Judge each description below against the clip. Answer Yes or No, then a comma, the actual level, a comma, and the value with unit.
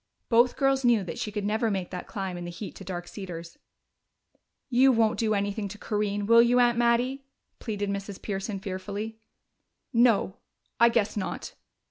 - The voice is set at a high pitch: Yes, high, 210 Hz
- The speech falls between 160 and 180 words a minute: Yes, average, 170 wpm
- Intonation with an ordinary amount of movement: Yes, average, 3.1 semitones